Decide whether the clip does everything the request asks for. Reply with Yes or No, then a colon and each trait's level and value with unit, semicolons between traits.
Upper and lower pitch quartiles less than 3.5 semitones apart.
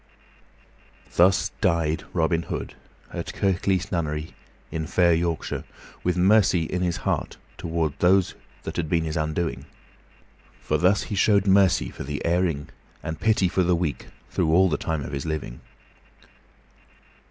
Yes: average, 2.7 semitones